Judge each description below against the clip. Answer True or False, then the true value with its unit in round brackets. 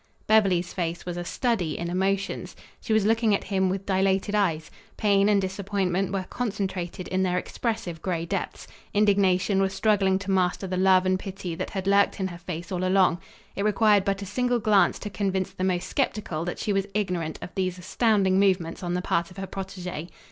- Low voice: False (190 Hz)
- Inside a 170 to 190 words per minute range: False (200 wpm)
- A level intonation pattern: True (1.9 semitones)